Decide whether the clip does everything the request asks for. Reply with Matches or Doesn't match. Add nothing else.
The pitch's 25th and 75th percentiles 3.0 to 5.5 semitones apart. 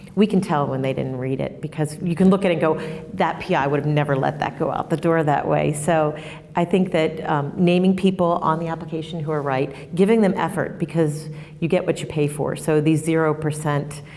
Doesn't match